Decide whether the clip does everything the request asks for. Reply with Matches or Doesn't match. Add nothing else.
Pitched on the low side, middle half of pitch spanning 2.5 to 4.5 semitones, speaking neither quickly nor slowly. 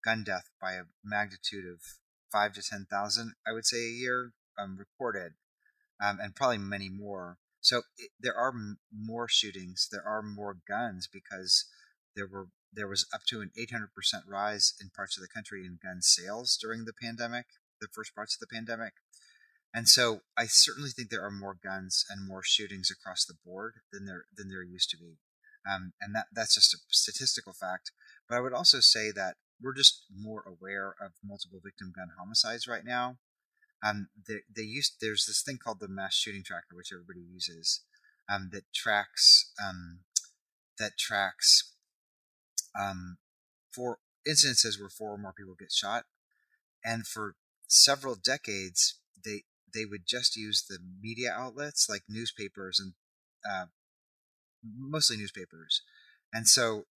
Matches